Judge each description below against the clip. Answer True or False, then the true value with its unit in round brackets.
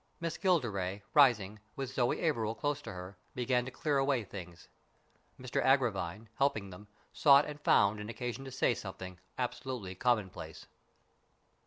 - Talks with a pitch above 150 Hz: False (120 Hz)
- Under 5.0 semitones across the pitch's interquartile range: False (5.3 semitones)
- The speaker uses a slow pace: False (145 wpm)